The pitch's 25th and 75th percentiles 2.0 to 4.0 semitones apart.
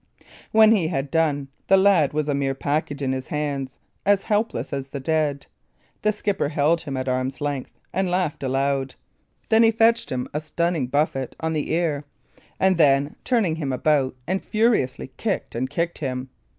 No: average, 4.7 semitones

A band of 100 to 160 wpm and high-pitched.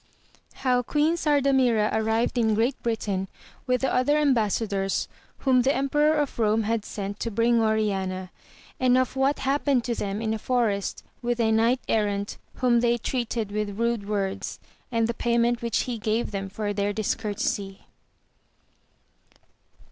Yes: average, 155 wpm; high, 230 Hz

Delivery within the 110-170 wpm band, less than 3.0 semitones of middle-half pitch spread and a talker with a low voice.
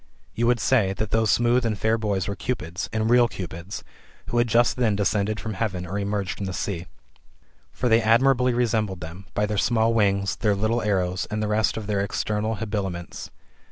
No: average, 195 wpm; narrow, 2.6 semitones; low, 105 Hz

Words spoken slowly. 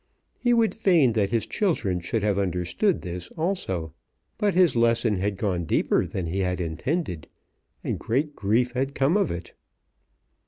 No: average, 160 wpm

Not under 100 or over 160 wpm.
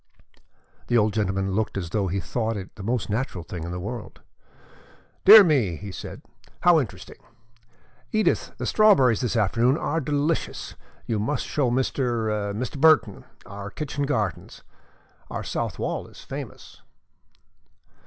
Yes: average, 145 wpm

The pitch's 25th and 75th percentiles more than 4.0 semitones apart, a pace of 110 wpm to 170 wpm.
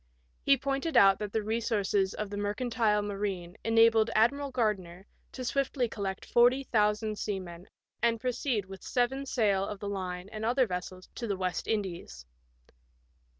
No: average, 3.6 semitones; average, 150 wpm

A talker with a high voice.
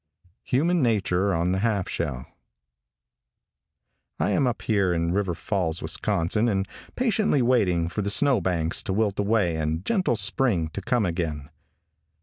No: low, 100 Hz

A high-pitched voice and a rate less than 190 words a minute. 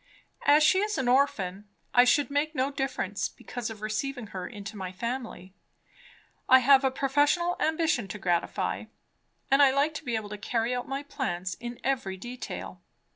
Yes: very high, 250 Hz; average, 175 wpm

